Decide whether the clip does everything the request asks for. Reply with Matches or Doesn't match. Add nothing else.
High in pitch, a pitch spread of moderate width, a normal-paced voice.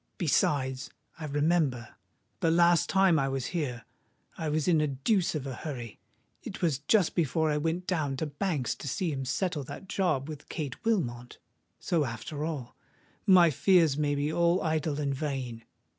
Doesn't match